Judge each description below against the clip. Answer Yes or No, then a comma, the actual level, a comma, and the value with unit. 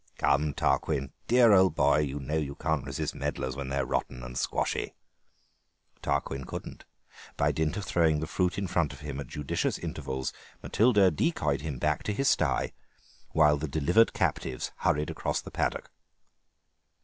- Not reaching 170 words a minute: Yes, average, 160 wpm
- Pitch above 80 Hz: No, very low, 75 Hz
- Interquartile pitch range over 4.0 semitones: Yes, average, 4.6 semitones